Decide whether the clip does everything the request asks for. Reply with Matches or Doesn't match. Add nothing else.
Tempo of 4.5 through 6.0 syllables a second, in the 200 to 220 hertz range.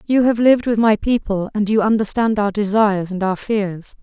Matches